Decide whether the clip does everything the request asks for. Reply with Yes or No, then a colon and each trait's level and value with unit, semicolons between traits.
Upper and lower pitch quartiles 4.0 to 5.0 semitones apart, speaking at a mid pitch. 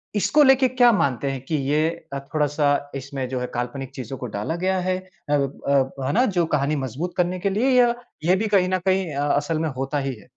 No: wide, 5.5 semitones; medium, 150 Hz